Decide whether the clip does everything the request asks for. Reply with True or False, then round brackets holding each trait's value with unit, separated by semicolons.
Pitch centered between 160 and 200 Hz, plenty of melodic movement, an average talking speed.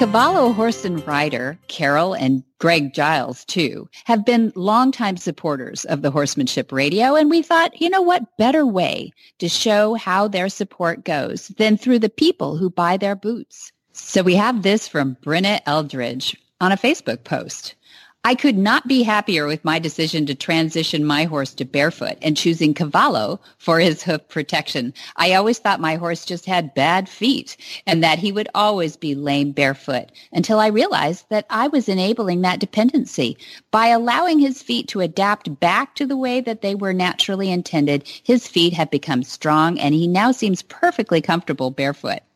True (185 Hz; 6.5 semitones; 175 wpm)